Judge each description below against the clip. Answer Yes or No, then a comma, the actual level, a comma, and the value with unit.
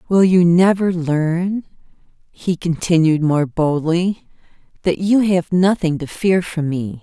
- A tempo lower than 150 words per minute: Yes, slow, 135 wpm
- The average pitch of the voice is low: No, medium, 170 Hz